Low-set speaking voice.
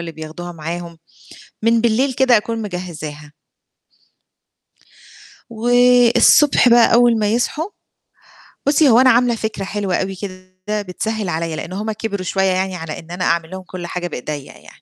No: high, 195 Hz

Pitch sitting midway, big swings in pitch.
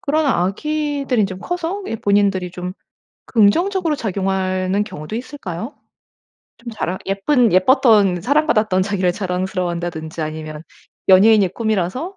No: high, 200 Hz; wide, 5.9 semitones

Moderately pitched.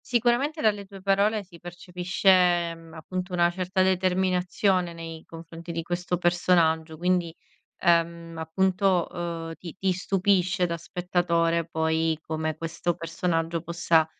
Yes: medium, 175 Hz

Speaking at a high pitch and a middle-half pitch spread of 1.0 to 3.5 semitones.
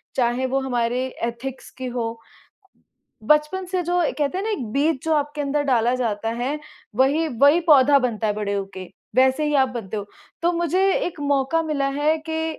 No: very high, 275 Hz; average, 4.5 semitones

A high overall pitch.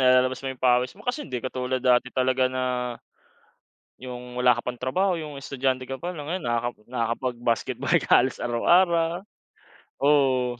No: low, 130 Hz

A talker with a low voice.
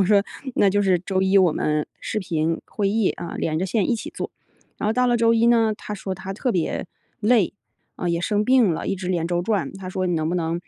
No: high, 190 Hz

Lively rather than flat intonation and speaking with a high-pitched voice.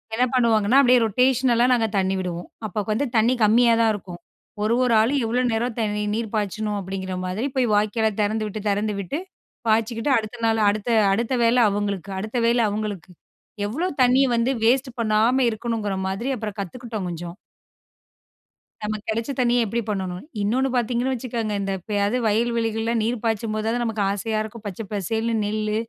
No: narrow, 2.5 semitones; high, 220 Hz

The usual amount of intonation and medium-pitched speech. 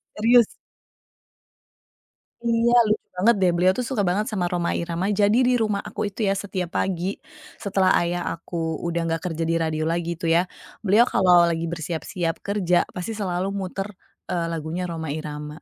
Yes: average, 3.1 semitones; medium, 180 Hz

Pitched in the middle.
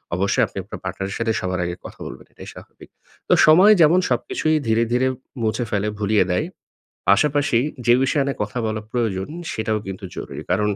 No: low, 110 Hz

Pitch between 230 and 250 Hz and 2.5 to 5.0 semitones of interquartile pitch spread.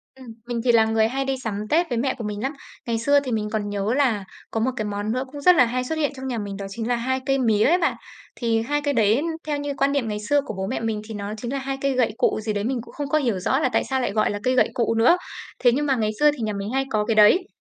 Yes: high, 240 Hz; average, 4.1 semitones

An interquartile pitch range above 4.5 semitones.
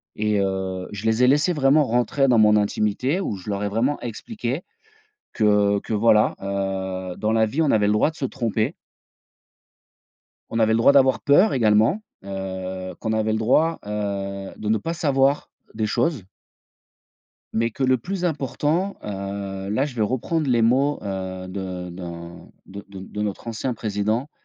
Yes: average, 5.2 semitones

